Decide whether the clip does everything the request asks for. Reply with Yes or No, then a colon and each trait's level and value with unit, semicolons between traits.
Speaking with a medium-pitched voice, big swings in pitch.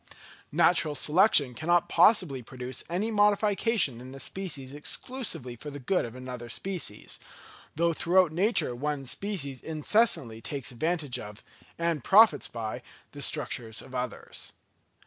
Yes: medium, 150 Hz; wide, 6.6 semitones